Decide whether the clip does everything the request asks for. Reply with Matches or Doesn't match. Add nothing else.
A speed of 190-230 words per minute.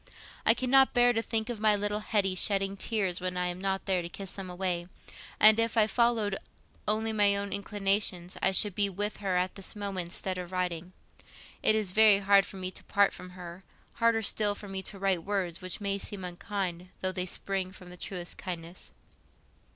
Matches